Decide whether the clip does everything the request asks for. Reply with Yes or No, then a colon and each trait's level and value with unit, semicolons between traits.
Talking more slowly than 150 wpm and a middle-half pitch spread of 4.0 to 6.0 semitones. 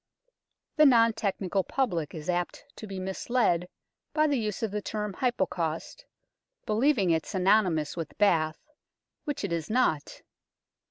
Yes: average, 140 wpm; average, 5.2 semitones